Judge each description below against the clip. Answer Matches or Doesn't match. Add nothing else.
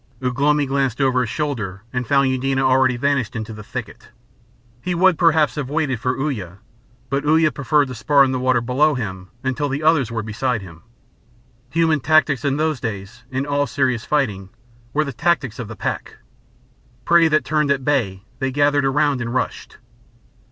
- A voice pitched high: Doesn't match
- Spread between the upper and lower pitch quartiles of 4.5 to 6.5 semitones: Doesn't match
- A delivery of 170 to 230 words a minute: Matches